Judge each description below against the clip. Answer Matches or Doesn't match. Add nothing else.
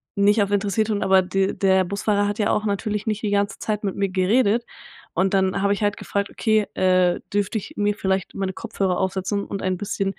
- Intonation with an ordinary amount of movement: Doesn't match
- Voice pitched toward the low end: Doesn't match